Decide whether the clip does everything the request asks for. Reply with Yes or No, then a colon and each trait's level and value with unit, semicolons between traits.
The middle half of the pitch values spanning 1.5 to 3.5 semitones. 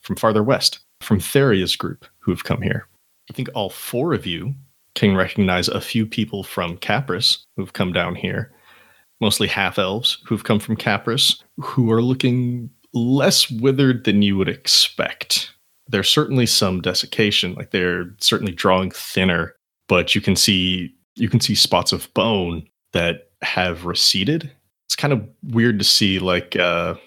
No: average, 4.7 semitones